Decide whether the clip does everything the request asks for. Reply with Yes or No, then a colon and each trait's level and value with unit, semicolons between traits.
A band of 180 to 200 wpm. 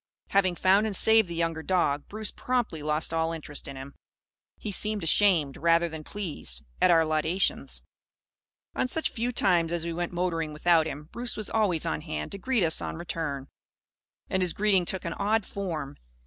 Yes: average, 190 wpm